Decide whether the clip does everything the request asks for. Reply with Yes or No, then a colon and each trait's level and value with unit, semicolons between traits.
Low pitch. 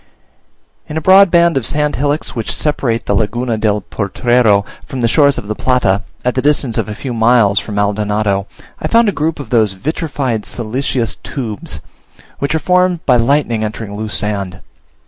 Yes: low, 120 Hz